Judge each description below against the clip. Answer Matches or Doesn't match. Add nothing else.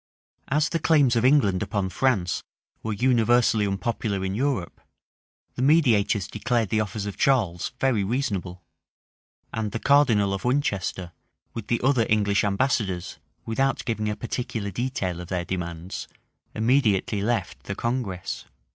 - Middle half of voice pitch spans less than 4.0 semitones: Doesn't match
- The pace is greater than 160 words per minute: Doesn't match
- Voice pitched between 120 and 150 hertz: Doesn't match